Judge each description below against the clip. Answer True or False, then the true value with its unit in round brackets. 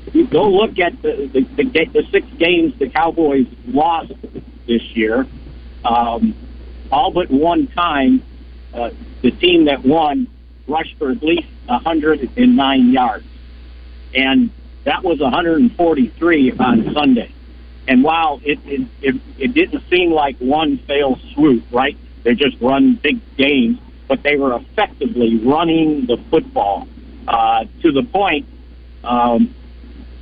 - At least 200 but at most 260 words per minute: False (135 wpm)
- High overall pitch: False (140 Hz)